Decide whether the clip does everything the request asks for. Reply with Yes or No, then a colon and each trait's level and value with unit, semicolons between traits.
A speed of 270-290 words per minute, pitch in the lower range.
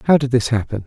Yes: fast, 280 wpm; low, 120 Hz